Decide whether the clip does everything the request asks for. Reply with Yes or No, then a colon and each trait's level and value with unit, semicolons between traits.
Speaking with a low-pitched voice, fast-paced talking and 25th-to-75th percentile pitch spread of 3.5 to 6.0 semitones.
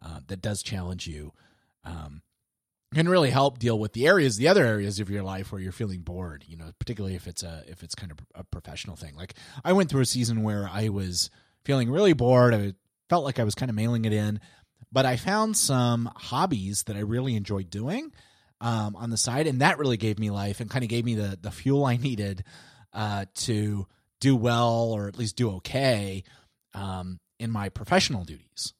Yes: low, 105 Hz; fast, 215 wpm; average, 4.3 semitones